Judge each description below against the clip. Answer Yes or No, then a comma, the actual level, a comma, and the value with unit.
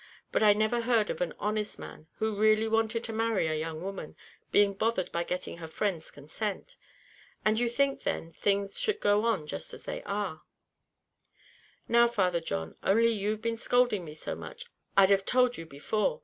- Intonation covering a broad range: No, average, 4.2 semitones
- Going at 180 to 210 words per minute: Yes, average, 185 wpm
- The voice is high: Yes, high, 210 Hz